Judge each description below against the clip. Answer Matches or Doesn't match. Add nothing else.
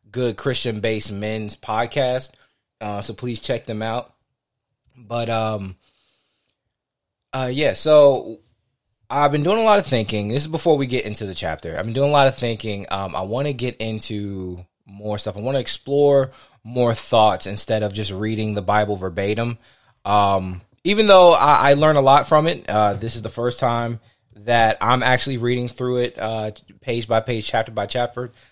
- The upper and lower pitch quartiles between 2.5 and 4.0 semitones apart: Matches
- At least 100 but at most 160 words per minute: Doesn't match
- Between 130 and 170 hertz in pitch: Doesn't match